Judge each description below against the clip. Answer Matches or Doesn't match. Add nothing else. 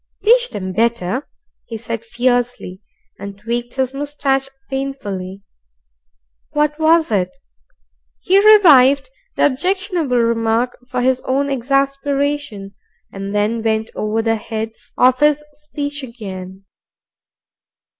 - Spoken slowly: Matches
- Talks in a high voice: Matches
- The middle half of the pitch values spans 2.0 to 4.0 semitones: Doesn't match